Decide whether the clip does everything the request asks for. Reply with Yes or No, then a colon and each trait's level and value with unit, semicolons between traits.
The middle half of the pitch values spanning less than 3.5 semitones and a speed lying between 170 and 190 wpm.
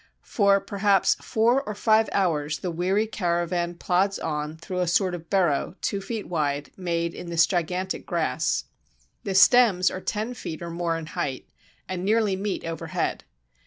No: average, 3.1 semitones; average, 160 wpm